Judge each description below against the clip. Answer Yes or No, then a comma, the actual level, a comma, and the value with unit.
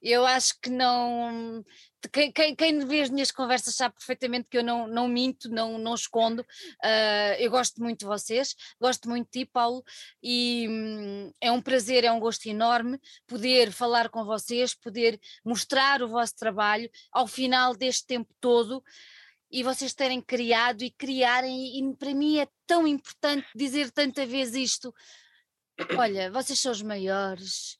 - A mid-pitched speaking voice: No, high, 245 Hz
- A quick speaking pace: No, average, 160 wpm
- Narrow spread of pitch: Yes, narrow, 2.1 semitones